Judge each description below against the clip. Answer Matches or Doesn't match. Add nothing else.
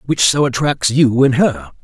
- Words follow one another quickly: Doesn't match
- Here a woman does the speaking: Doesn't match